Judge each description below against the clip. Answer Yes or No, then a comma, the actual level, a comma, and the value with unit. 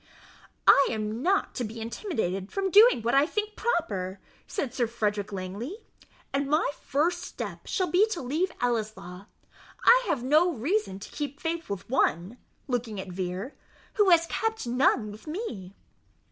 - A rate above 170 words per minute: No, average, 160 wpm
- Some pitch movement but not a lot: No, wide, 8.6 semitones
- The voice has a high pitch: Yes, very high, 255 Hz